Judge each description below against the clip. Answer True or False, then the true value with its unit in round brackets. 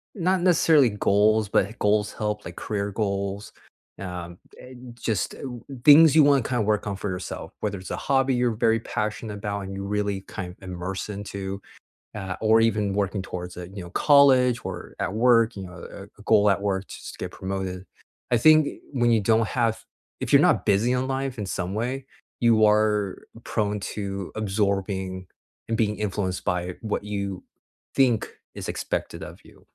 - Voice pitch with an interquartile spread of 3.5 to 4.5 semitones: False (3.1 semitones)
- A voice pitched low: True (105 Hz)